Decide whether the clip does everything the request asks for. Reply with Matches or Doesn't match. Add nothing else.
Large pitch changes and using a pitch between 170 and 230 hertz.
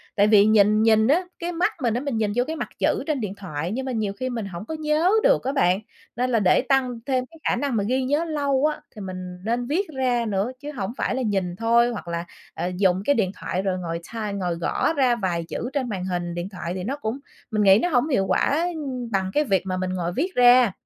Matches